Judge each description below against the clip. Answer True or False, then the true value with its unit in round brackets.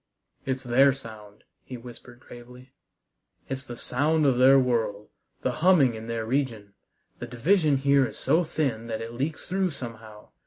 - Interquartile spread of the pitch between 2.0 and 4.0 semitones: True (3.3 semitones)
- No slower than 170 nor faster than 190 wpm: False (160 wpm)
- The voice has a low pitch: True (125 Hz)